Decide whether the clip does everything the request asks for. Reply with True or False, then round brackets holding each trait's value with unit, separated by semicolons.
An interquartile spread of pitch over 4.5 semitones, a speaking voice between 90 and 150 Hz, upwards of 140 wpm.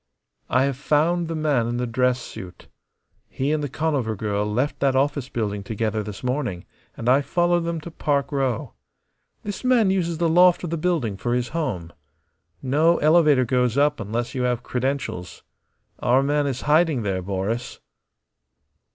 True (4.9 semitones; 135 Hz; 170 wpm)